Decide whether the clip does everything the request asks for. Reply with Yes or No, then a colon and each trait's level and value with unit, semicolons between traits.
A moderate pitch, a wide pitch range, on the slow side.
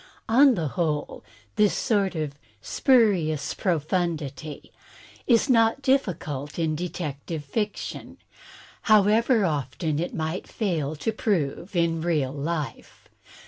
Yes: medium, 170 Hz; wide, 5.8 semitones; slow, 110 wpm